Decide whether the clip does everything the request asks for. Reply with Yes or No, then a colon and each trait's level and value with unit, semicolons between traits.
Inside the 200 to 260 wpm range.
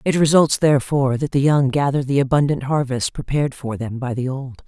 Yes: fast, 205 wpm